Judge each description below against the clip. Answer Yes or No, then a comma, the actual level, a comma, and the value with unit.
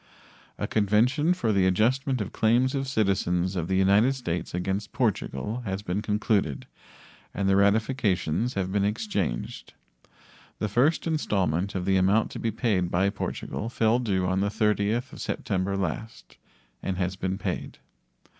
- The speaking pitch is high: No, low, 100 Hz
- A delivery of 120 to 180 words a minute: Yes, average, 155 wpm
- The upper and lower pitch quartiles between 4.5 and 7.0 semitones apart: No, average, 3.4 semitones